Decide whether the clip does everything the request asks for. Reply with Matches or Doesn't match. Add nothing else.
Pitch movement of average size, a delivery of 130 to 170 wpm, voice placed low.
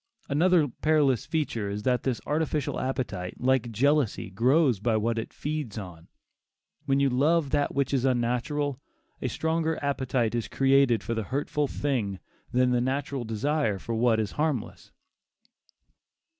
Matches